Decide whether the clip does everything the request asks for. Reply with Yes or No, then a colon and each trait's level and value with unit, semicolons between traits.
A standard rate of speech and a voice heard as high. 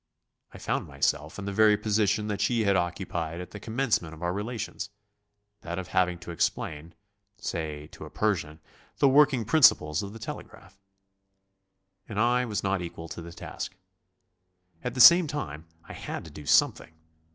No: average, 170 wpm; low, 100 Hz